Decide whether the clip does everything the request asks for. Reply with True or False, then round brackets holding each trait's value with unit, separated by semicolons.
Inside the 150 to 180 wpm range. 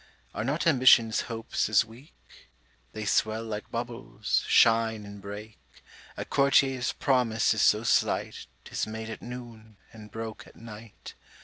False (140 wpm)